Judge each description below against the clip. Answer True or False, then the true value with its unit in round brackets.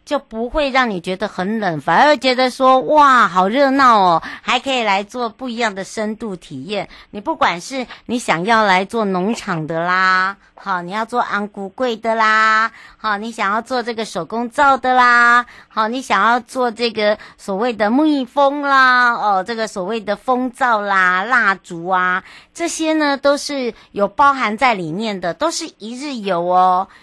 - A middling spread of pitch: True (4.9 semitones)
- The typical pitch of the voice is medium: False (225 Hz)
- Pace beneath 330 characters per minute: True (240 characters per minute)